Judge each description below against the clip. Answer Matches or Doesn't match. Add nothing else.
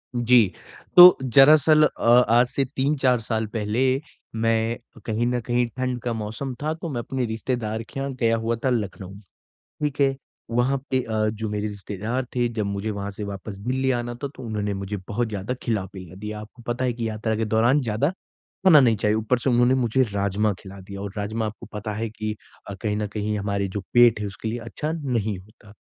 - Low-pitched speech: Matches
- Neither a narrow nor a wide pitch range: Matches